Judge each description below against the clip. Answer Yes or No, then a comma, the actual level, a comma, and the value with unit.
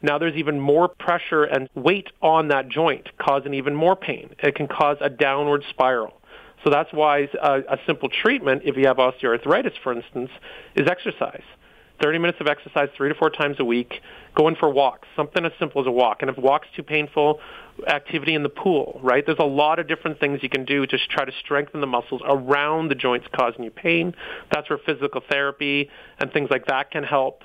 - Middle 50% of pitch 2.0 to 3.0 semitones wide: Yes, narrow, 2.4 semitones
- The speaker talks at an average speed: No, fast, 210 wpm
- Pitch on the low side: No, medium, 145 Hz